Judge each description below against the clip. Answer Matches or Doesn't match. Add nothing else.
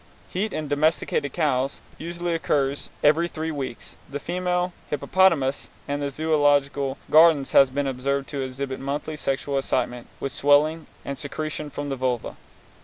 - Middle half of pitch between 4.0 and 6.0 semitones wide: Doesn't match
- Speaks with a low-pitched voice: Doesn't match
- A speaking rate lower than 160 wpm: Matches